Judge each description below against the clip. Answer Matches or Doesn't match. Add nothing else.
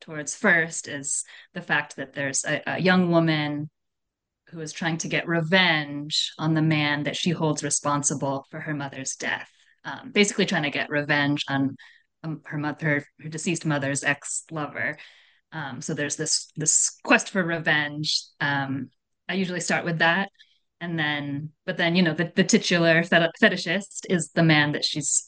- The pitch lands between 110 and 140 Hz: Doesn't match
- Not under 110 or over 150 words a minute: Doesn't match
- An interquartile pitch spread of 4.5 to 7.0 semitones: Doesn't match